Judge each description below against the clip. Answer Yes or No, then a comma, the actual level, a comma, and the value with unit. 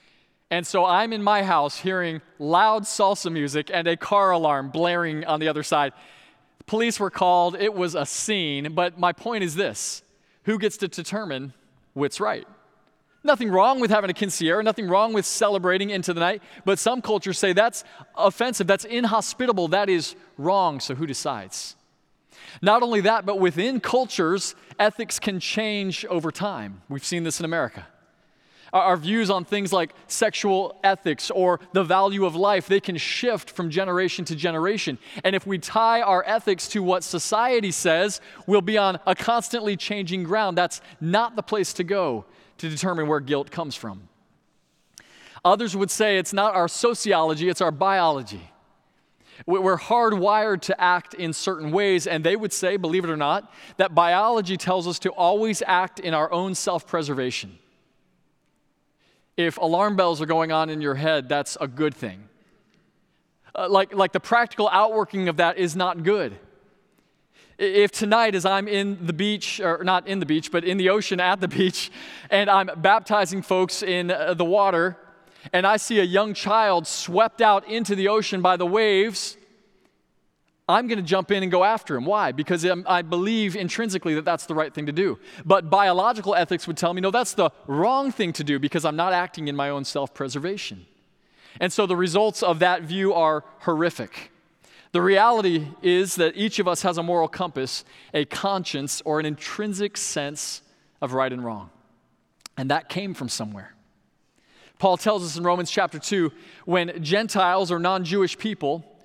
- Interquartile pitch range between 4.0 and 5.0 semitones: No, average, 3.5 semitones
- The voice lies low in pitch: No, medium, 185 Hz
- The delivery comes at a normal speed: Yes, average, 175 wpm